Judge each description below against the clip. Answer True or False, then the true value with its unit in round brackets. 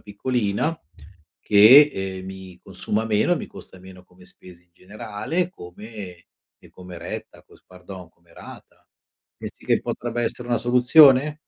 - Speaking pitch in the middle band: False (105 Hz)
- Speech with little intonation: False (5.0 semitones)